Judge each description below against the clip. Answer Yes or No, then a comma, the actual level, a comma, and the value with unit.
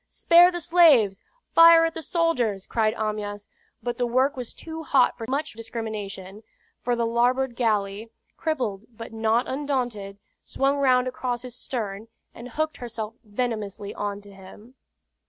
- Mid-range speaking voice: No, high, 235 Hz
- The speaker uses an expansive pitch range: No, average, 4.0 semitones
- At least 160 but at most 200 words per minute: No, average, 150 wpm